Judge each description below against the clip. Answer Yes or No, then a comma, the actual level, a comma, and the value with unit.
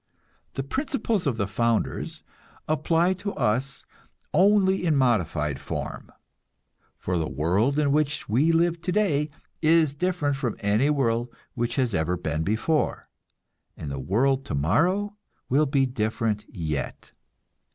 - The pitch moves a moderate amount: No, wide, 7.5 semitones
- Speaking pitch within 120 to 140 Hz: Yes, low, 135 Hz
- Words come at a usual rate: No, slow, 130 wpm